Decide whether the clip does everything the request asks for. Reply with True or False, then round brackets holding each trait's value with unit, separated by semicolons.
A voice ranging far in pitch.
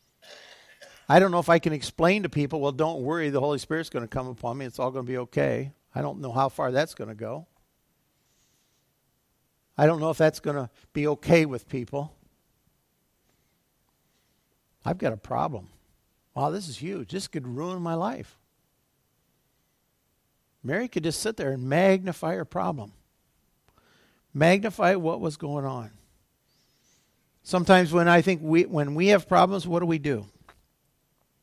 False (4.4 semitones)